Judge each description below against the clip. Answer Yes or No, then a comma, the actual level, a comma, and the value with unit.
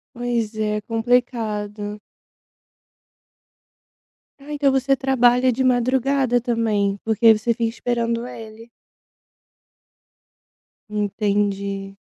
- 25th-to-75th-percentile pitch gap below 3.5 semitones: Yes, average, 2.7 semitones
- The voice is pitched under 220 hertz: No, high, 230 Hz